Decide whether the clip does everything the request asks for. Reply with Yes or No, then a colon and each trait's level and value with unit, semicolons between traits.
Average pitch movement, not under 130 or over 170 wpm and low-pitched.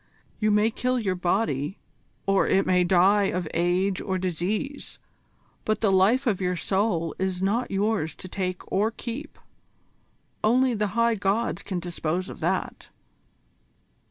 No: average, 3.3 semitones; average, 145 wpm; high, 195 Hz